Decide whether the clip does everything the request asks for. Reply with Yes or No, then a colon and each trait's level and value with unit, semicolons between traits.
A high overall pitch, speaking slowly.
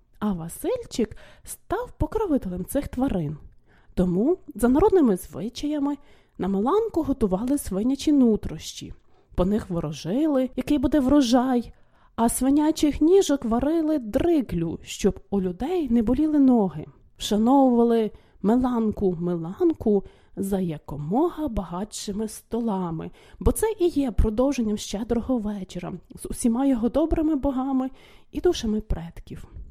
Yes: high, 245 Hz; slow, 105 wpm